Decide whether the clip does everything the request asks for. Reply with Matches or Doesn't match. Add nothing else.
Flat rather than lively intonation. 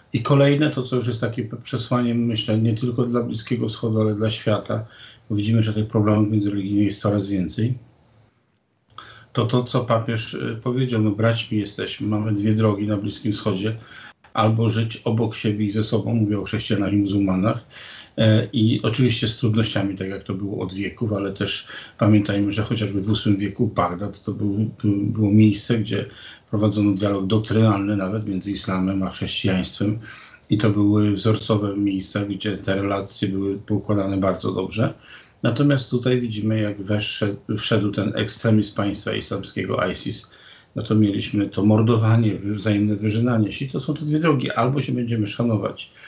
Matches